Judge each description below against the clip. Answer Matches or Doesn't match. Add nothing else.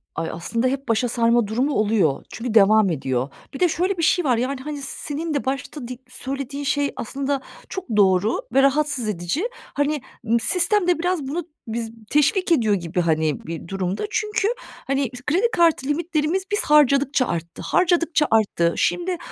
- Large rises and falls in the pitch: Matches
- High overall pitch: Matches